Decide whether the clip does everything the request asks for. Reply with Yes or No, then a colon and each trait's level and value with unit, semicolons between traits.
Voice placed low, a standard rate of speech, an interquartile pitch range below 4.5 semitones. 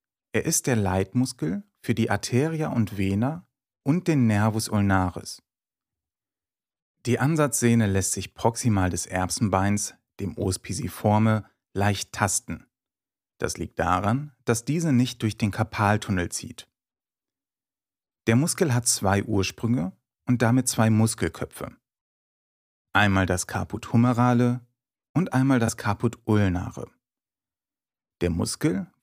No: low, 110 Hz; slow, 110 wpm; average, 3.9 semitones